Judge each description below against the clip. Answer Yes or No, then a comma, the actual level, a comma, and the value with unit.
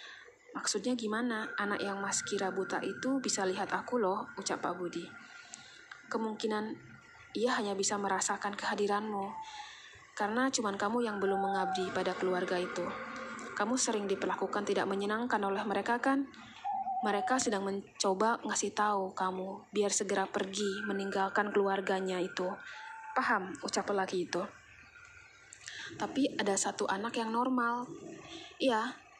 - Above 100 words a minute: Yes, average, 125 wpm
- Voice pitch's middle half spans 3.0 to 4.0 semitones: Yes, average, 3.7 semitones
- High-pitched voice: Yes, high, 205 Hz